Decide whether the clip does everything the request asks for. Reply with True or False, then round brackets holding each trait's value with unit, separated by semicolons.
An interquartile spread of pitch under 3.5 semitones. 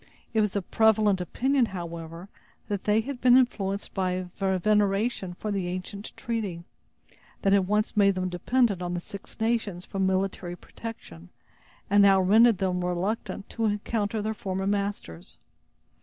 True (2.9 semitones)